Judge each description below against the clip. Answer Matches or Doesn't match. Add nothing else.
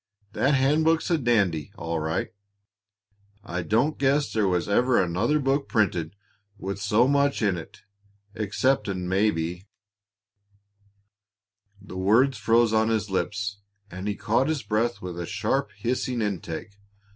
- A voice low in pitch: Matches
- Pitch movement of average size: Matches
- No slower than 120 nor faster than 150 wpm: Matches